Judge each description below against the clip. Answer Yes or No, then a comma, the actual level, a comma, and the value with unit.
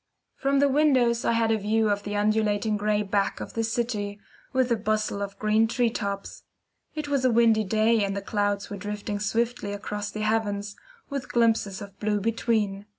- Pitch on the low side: No, high, 215 Hz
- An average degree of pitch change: No, narrow, 2.1 semitones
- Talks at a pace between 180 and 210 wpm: Yes, average, 190 wpm